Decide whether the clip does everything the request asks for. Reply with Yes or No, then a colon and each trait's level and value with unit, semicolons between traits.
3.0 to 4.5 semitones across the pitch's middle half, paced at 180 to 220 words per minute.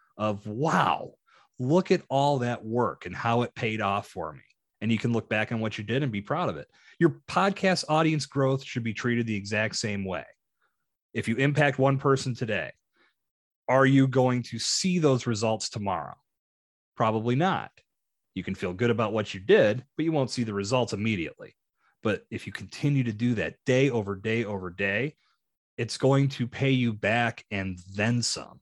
Yes: average, 3.9 semitones; average, 190 wpm